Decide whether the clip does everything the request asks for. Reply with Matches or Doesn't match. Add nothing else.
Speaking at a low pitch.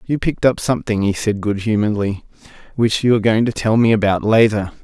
Matches